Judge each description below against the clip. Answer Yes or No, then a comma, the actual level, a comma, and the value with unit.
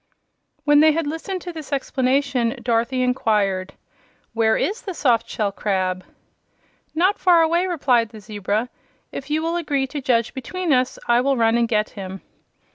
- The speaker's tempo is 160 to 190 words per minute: Yes, average, 165 wpm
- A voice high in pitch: Yes, very high, 255 Hz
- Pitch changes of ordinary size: No, wide, 5.8 semitones